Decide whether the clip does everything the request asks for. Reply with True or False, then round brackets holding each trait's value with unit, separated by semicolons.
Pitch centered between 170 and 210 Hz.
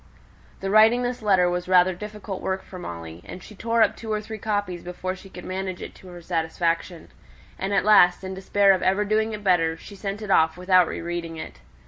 True (190 Hz)